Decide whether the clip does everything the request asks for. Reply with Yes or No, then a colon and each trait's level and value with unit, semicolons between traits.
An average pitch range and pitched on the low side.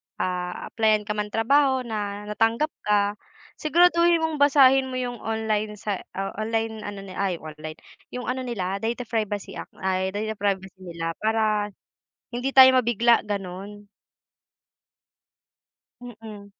No: average, 3.4 semitones; high, 215 Hz